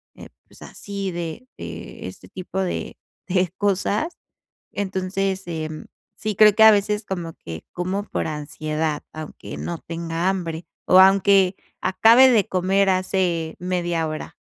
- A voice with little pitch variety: No, average, 3.1 semitones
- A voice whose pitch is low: No, medium, 185 Hz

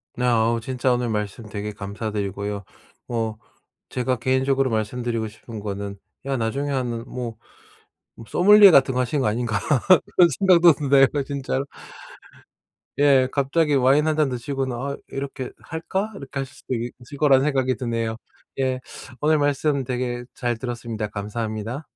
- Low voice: Yes, low, 125 Hz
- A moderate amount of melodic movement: Yes, average, 3.5 semitones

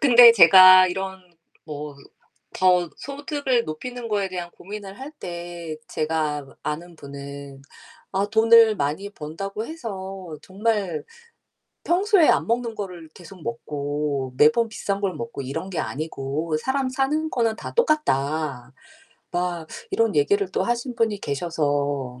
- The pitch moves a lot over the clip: Yes, wide, 7.0 semitones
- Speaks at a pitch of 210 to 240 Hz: No, medium, 185 Hz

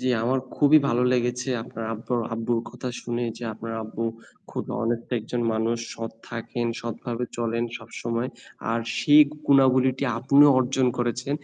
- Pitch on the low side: Yes, low, 120 Hz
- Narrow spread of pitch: Yes, narrow, 1.8 semitones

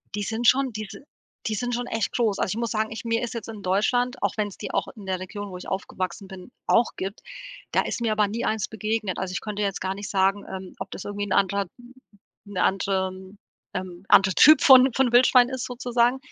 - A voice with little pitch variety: No, average, 3.6 semitones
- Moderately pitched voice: No, high, 210 Hz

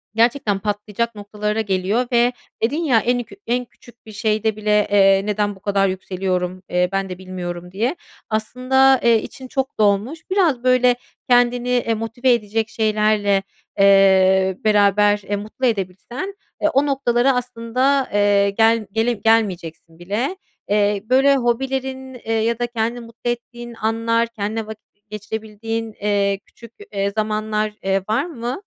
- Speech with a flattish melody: No, average, 3.2 semitones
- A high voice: Yes, high, 220 Hz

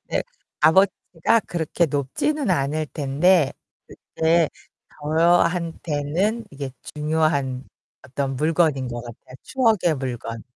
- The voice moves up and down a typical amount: Yes, average, 4.2 semitones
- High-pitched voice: No, medium, 155 Hz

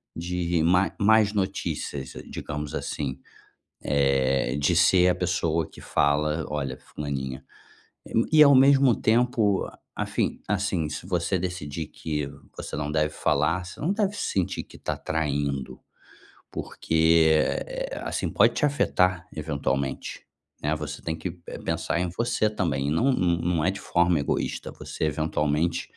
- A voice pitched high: No, very low, 85 Hz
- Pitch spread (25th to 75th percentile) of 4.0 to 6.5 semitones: Yes, average, 4.3 semitones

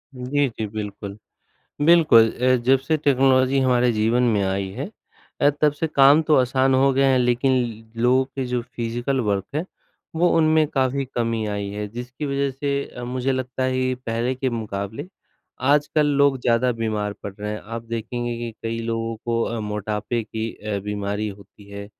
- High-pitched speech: No, low, 120 Hz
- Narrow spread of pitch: No, average, 3.3 semitones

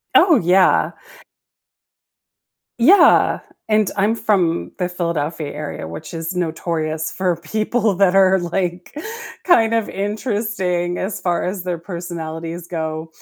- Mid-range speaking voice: Yes, medium, 180 Hz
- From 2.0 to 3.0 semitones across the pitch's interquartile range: No, average, 3.5 semitones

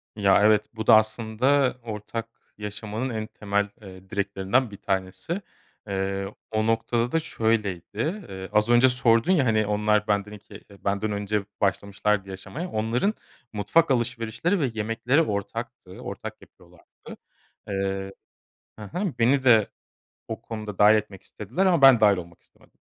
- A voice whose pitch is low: Yes, low, 110 Hz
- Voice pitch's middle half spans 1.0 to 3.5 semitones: Yes, average, 2.9 semitones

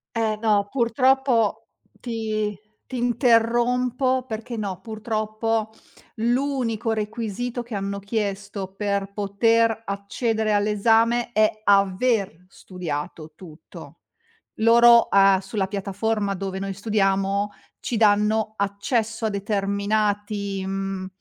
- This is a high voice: Yes, high, 215 Hz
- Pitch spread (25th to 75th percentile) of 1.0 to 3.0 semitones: Yes, narrow, 2.5 semitones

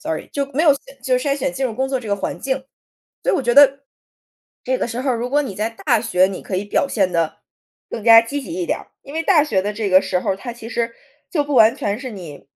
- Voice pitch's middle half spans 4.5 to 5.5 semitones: Yes, average, 5.1 semitones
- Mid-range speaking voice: No, high, 240 Hz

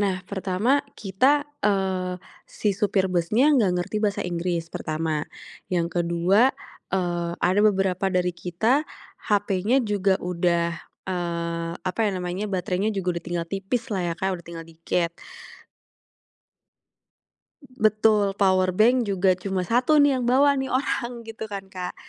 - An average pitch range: Yes, average, 3.2 semitones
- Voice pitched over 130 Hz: Yes, high, 190 Hz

